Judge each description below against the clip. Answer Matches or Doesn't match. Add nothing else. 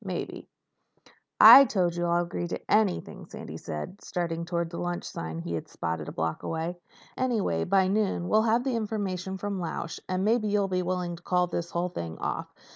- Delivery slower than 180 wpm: Doesn't match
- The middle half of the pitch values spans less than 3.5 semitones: Matches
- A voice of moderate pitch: Matches